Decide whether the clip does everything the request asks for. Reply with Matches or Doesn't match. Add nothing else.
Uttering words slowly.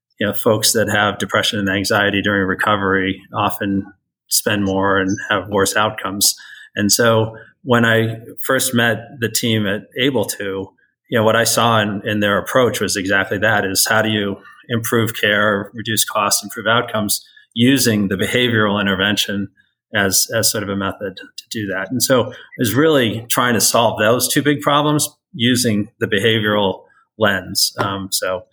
Doesn't match